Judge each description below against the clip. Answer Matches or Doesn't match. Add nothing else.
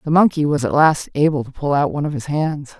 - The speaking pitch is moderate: Matches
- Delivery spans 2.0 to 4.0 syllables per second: Doesn't match